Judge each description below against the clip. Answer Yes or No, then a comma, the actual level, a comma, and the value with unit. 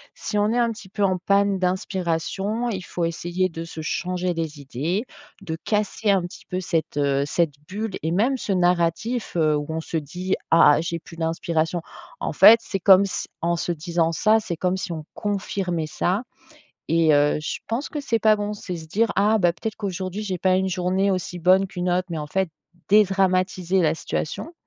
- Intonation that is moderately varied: Yes, average, 3.3 semitones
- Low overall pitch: No, medium, 185 Hz